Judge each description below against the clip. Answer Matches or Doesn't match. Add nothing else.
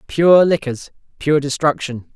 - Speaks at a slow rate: Matches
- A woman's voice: Doesn't match